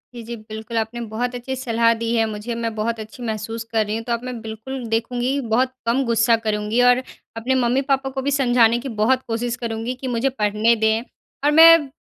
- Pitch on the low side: No, high, 235 Hz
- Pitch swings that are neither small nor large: No, narrow, 2.2 semitones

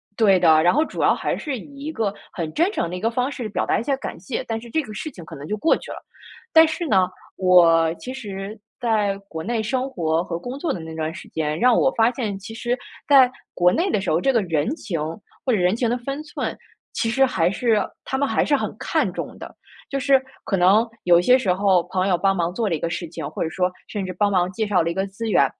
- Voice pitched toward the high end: Yes, high, 205 Hz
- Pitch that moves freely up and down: Yes, wide, 6.0 semitones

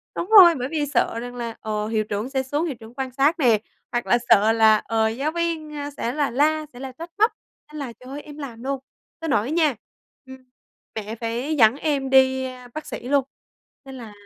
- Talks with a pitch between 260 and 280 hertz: Yes, very high, 265 Hz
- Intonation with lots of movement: No, average, 4.6 semitones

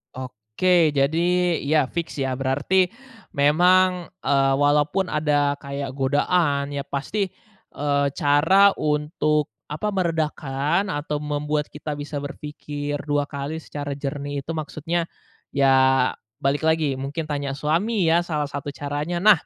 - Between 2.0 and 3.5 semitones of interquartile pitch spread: Yes, narrow, 2.6 semitones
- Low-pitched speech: No, medium, 150 Hz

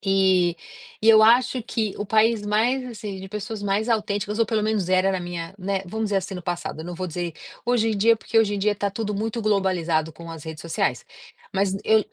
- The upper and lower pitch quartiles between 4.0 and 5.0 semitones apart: No, average, 3.0 semitones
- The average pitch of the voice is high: Yes, high, 205 Hz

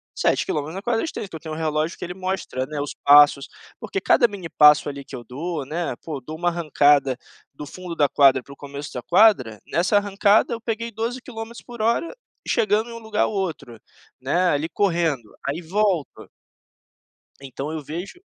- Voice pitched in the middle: Yes, medium, 165 Hz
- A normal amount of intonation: No, wide, 6.2 semitones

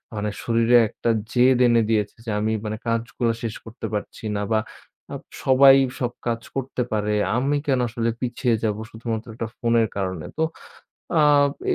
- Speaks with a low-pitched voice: Yes, low, 115 Hz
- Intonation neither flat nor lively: No, narrow, 2.1 semitones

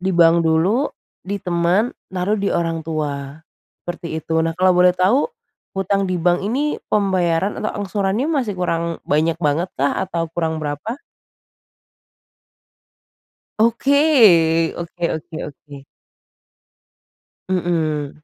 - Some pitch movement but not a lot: Yes, average, 3.5 semitones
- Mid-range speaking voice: Yes, medium, 175 Hz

